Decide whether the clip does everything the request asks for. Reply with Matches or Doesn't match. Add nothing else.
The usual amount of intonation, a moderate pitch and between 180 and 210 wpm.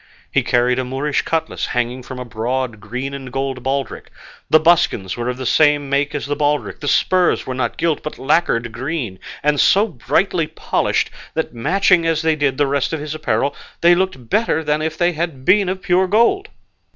Matches